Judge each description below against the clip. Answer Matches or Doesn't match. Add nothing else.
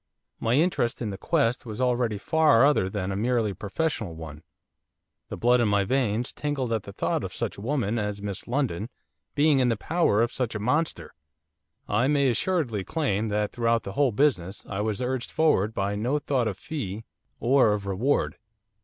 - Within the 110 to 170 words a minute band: Doesn't match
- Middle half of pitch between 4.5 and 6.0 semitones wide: Matches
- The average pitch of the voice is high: Doesn't match